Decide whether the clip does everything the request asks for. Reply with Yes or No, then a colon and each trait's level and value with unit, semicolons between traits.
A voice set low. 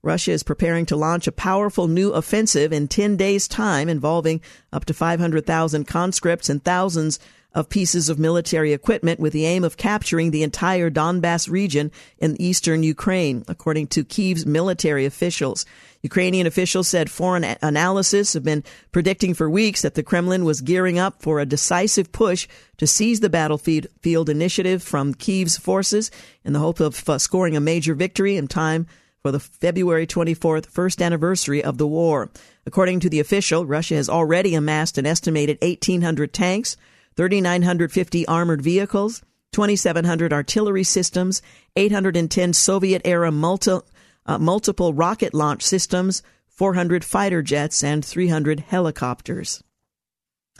No: medium, 170 Hz